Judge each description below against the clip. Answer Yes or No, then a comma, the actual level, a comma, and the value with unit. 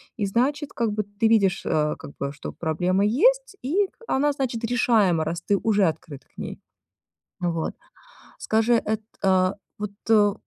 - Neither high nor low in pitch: No, high, 210 Hz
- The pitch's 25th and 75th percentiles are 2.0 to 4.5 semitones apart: No, average, 5.1 semitones